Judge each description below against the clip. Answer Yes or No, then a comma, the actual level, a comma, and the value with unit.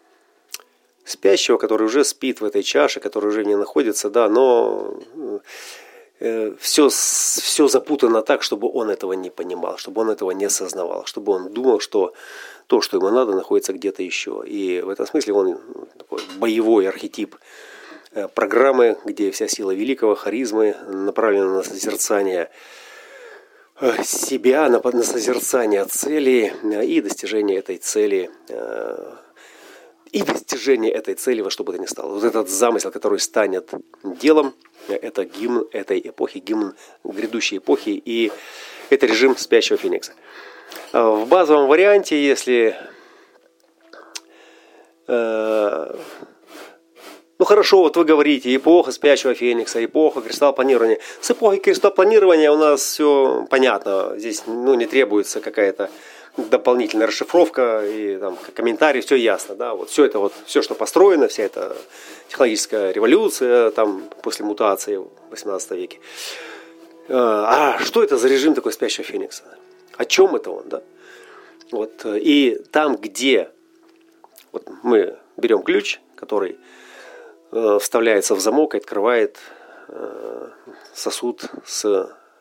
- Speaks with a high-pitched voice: Yes, very high, 395 Hz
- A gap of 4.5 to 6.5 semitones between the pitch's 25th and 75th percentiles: Yes, average, 5.2 semitones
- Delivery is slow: No, average, 125 wpm